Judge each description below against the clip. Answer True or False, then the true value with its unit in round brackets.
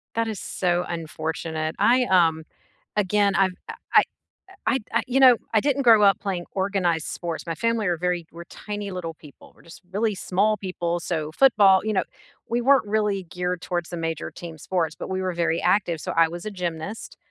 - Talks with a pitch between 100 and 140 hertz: False (185 Hz)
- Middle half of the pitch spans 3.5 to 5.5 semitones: True (3.8 semitones)